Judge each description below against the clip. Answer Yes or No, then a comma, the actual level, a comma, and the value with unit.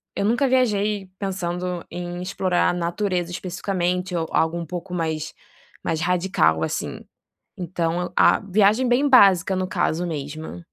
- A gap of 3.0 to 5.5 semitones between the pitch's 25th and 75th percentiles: No, narrow, 2.5 semitones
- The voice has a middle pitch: Yes, medium, 180 Hz